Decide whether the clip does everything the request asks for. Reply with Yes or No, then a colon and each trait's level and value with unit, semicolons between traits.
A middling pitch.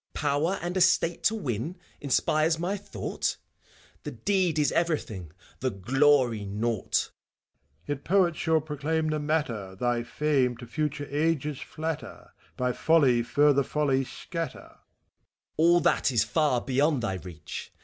Yes: medium, 145 Hz